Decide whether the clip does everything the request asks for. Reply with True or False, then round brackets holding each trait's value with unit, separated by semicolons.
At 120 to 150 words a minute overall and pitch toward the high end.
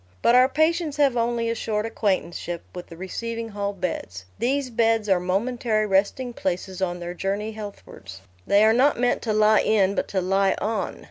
False (185 wpm; 215 Hz)